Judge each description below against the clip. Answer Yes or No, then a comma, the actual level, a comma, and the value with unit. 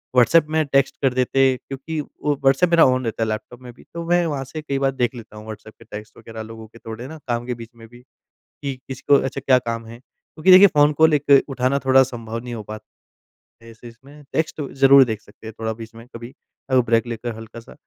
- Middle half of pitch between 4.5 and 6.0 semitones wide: No, average, 3.3 semitones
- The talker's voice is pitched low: Yes, low, 125 Hz